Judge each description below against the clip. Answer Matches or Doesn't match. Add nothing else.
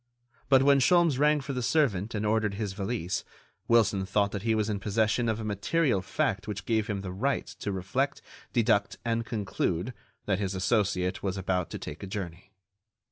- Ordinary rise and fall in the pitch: Matches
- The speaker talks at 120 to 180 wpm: Doesn't match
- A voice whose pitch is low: Matches